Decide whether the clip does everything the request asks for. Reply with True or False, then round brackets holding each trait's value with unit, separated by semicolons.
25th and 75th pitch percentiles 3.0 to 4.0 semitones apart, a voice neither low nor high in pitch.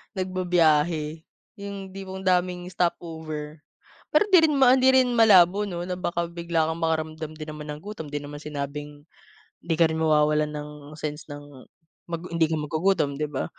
True (3.3 semitones; 160 Hz)